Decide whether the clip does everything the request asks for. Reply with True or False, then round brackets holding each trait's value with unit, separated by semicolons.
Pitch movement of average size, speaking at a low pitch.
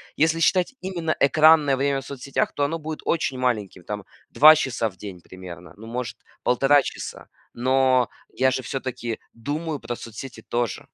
True (4.2 semitones; 130 Hz)